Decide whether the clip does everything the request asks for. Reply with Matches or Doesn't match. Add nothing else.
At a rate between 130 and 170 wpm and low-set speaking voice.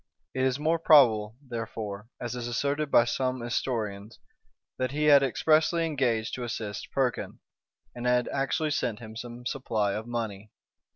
Matches